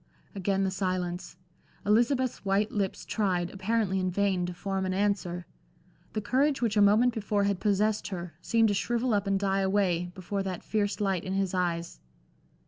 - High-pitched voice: Yes, high, 195 Hz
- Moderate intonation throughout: No, narrow, 2.2 semitones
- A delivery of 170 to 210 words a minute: Yes, average, 175 wpm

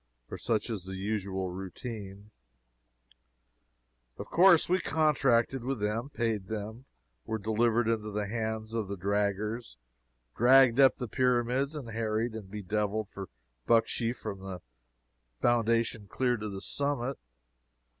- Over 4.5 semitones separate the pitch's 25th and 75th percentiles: No, average, 2.9 semitones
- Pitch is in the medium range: No, low, 110 Hz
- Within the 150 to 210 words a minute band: No, slow, 135 wpm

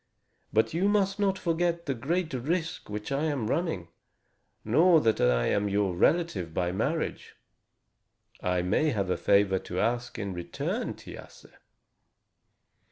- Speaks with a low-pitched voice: Yes, low, 120 Hz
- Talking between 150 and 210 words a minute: No, average, 140 wpm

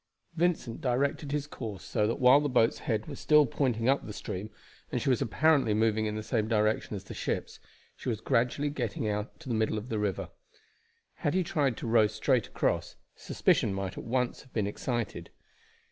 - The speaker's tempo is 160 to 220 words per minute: Yes, average, 200 wpm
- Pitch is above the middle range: No, low, 115 Hz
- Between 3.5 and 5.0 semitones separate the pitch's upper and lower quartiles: Yes, average, 4.3 semitones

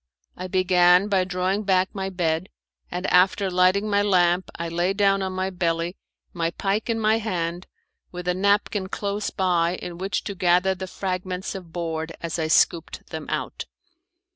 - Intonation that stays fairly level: Yes, narrow, 1.8 semitones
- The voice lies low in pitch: No, medium, 185 Hz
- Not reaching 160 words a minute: No, average, 170 wpm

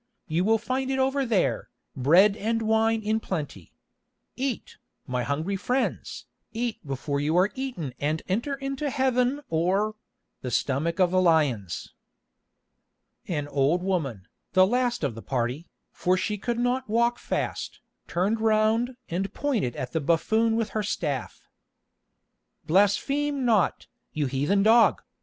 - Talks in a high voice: Yes, high, 200 Hz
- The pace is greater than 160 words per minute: No, average, 140 wpm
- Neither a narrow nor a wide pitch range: No, wide, 7.2 semitones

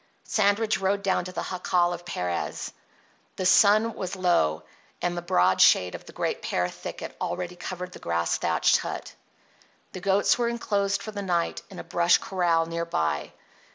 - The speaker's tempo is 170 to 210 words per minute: Yes, average, 175 wpm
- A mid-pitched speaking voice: Yes, medium, 180 Hz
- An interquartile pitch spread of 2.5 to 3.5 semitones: Yes, average, 2.9 semitones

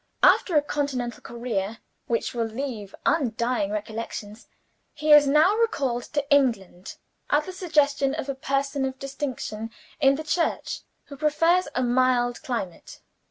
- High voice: Yes, very high, 265 Hz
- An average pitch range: Yes, average, 3.9 semitones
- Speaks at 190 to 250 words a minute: No, average, 140 wpm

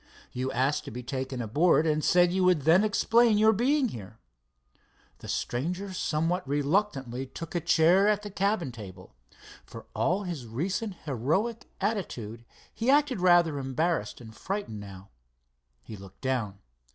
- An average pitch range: No, wide, 7.8 semitones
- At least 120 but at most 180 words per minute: Yes, average, 150 wpm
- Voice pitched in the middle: Yes, medium, 160 Hz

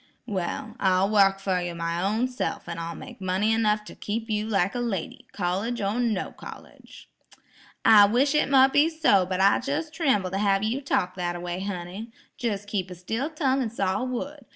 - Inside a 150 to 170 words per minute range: No, average, 200 wpm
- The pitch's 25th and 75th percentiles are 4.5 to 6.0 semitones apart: Yes, average, 4.8 semitones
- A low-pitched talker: No, high, 210 Hz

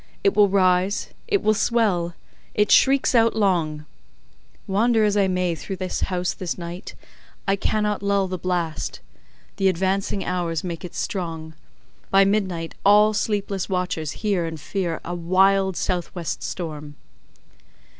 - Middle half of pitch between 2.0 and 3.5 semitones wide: Yes, average, 2.8 semitones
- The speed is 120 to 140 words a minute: Yes, slow, 135 wpm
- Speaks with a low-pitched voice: No, high, 190 Hz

